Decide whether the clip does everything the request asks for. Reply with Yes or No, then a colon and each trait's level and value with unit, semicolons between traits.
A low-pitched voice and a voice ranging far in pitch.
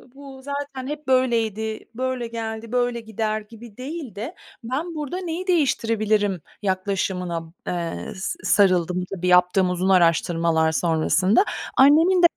No: high, 220 Hz; wide, 6.4 semitones